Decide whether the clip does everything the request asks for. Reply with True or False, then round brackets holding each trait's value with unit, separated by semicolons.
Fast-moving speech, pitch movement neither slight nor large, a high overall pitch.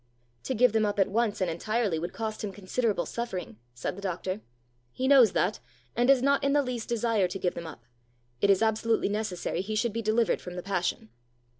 True (210 wpm; 4.0 semitones; 215 Hz)